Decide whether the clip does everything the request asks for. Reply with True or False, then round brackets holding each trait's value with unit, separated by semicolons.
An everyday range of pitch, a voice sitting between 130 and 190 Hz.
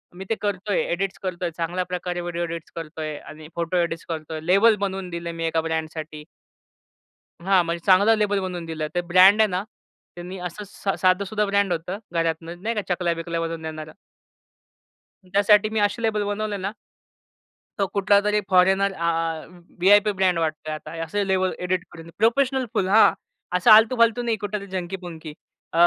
True (3.3 semitones; 185 Hz)